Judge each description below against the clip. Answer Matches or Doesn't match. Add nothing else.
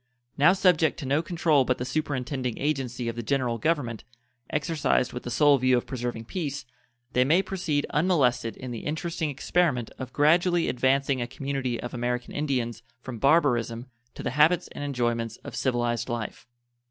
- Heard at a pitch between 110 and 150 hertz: Matches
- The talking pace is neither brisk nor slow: Matches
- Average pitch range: Matches